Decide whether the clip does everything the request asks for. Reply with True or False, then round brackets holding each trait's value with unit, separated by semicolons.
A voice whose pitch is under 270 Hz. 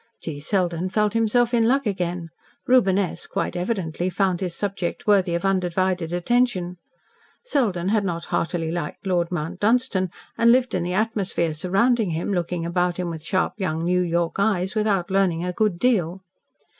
True (185 Hz)